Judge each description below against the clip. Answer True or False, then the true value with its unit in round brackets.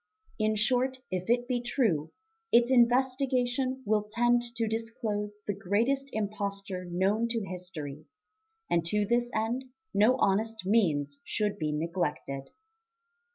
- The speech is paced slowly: True (125 wpm)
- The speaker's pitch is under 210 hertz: False (215 Hz)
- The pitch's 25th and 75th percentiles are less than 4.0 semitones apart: False (4.5 semitones)